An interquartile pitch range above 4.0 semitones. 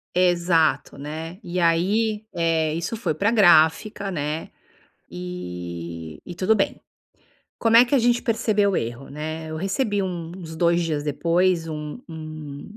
Yes: average, 4.4 semitones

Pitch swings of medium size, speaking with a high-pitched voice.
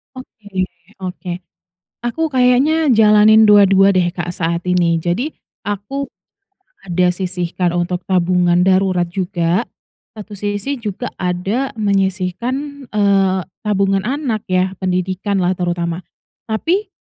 Yes: average, 3.5 semitones; high, 195 Hz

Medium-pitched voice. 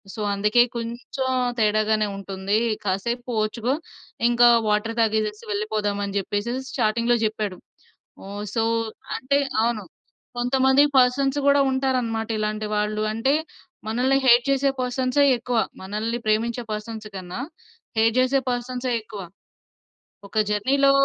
No: high, 230 Hz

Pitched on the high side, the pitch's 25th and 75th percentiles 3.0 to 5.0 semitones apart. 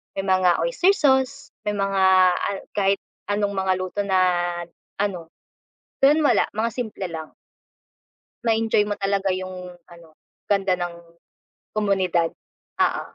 No: high, 195 Hz; narrow, 2.6 semitones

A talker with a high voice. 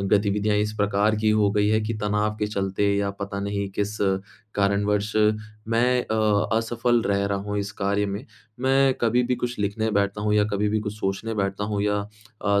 No: low, 105 Hz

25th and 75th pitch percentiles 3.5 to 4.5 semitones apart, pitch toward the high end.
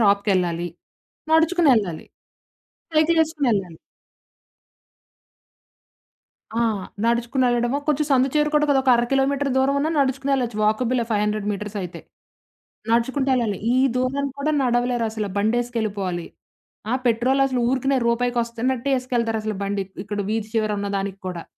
Yes: average, 4.2 semitones; high, 240 Hz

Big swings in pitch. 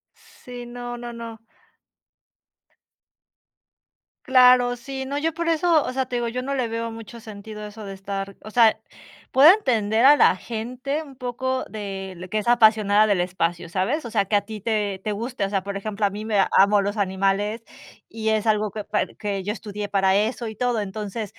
No: average, 3.3 semitones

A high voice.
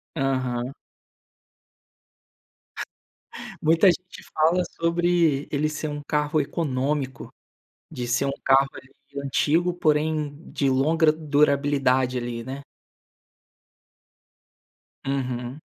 No: medium, 145 Hz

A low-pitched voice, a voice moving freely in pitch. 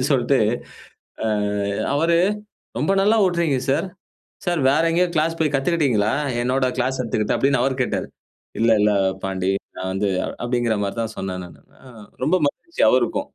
Yes: low, 130 Hz; wide, 6.7 semitones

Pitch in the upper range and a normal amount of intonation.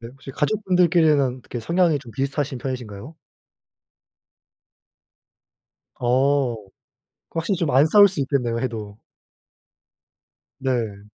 No: low, 135 Hz; average, 4.8 semitones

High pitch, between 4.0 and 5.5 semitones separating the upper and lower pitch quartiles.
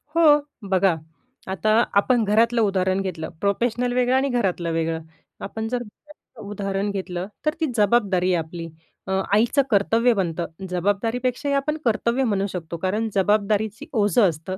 Yes: high, 205 Hz; average, 4.3 semitones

